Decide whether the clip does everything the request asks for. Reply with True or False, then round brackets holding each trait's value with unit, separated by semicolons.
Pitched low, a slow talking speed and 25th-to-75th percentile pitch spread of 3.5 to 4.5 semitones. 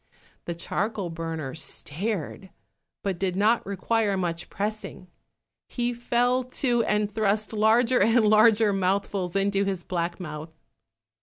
False (200 Hz; 125 wpm; 3.8 semitones)